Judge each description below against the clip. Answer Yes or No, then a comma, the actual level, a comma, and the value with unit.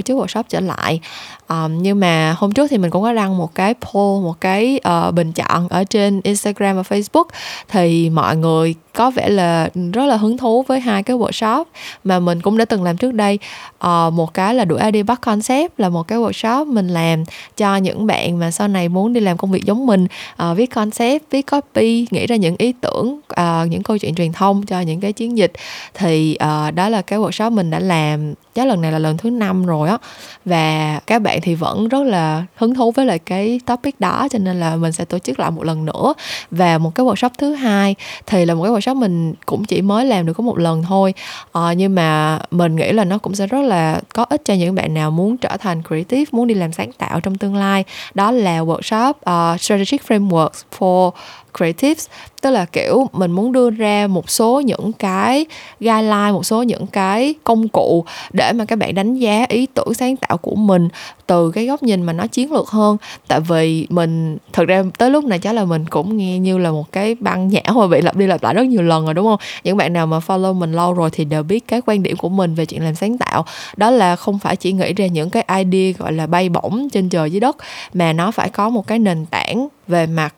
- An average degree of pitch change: Yes, average, 5.0 semitones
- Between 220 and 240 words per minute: Yes, average, 235 wpm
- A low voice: No, high, 195 Hz